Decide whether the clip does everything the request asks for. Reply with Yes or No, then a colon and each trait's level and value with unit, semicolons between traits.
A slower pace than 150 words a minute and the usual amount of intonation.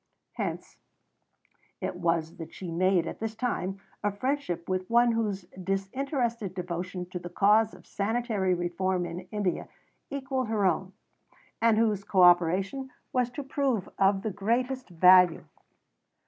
Yes: average, 140 wpm; average, 4.3 semitones